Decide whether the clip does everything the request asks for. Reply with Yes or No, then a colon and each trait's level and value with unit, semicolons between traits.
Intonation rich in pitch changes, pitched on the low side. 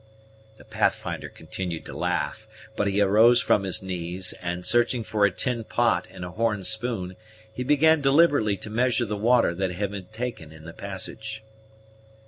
No: average, 4.4 semitones; low, 105 Hz